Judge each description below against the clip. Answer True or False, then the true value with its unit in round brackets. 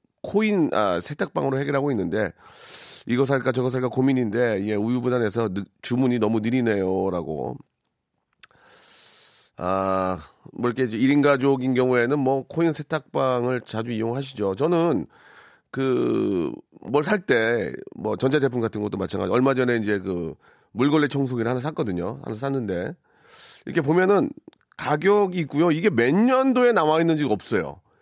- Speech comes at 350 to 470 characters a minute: False (305 characters per minute)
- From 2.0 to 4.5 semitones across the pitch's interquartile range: False (5.2 semitones)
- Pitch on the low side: True (130 Hz)